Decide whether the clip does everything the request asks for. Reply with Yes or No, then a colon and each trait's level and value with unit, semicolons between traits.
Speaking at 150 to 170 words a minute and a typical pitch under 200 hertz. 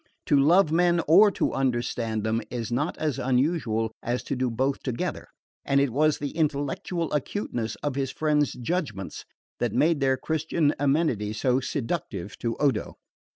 Yes: average, 155 wpm; medium, 140 Hz